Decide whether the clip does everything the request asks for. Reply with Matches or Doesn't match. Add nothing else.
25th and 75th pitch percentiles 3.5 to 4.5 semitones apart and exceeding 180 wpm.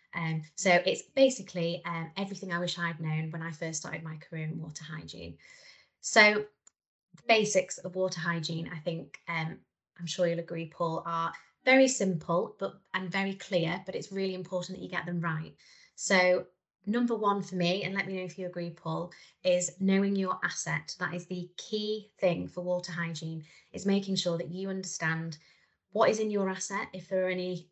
Doesn't match